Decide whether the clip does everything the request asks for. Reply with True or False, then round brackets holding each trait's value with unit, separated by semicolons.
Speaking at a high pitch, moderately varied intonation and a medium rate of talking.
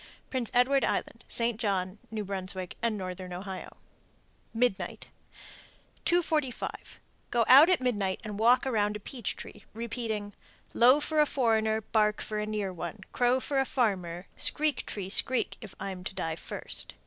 True (220 Hz; 4.3 semitones; 150 wpm)